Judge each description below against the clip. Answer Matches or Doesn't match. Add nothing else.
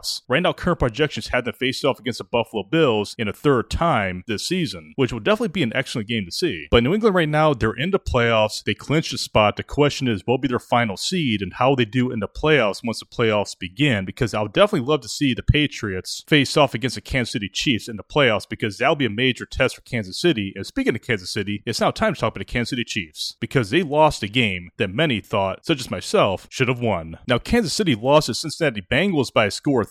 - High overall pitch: Doesn't match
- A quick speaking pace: Matches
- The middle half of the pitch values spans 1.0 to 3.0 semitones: Doesn't match